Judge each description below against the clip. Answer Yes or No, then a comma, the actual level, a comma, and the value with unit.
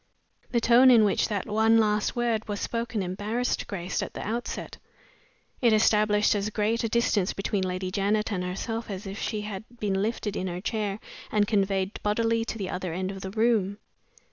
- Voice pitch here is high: Yes, high, 210 Hz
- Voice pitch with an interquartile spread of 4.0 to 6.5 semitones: No, narrow, 2.6 semitones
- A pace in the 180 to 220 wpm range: Yes, average, 190 wpm